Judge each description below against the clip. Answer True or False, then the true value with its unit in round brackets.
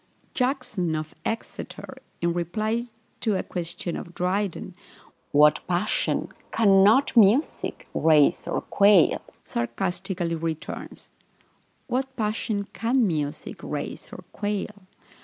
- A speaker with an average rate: False (100 wpm)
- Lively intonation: False (4.3 semitones)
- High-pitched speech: True (195 Hz)